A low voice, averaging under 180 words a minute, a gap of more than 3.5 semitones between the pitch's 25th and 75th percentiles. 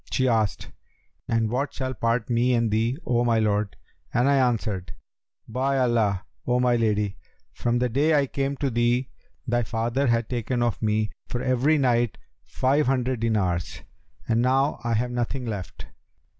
No: low, 120 Hz; average, 165 wpm; narrow, 2.4 semitones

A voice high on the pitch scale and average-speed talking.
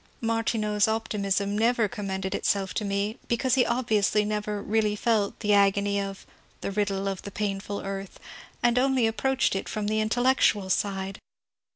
Yes: high, 210 Hz; average, 160 wpm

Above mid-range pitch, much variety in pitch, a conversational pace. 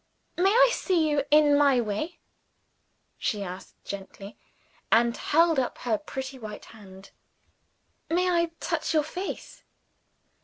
No: very high, 285 Hz; wide, 7.5 semitones; slow, 125 wpm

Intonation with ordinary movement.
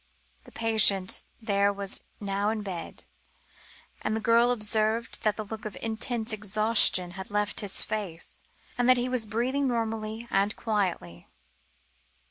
No: narrow, 2.1 semitones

